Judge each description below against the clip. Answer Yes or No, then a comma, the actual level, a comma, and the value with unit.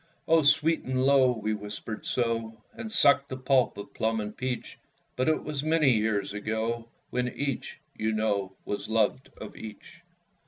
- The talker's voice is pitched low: Yes, low, 115 Hz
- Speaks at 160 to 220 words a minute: Yes, average, 165 wpm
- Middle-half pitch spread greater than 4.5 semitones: No, average, 4.1 semitones